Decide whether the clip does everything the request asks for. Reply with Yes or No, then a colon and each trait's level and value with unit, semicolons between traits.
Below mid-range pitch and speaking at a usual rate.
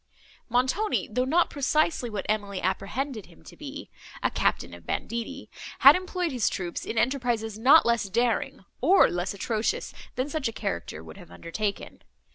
No: high, 230 Hz; average, 150 wpm